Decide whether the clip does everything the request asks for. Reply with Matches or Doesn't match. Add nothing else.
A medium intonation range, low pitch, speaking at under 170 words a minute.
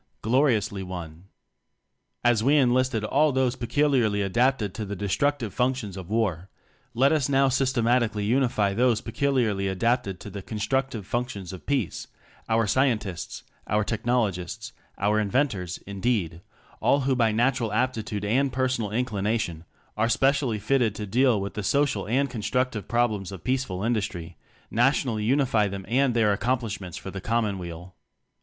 Matches